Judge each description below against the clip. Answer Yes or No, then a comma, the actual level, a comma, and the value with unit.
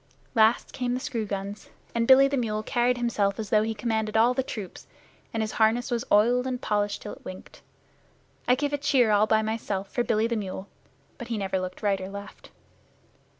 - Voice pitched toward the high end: Yes, high, 220 Hz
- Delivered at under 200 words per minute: No, fast, 205 wpm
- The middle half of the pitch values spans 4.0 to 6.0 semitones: No, average, 3.0 semitones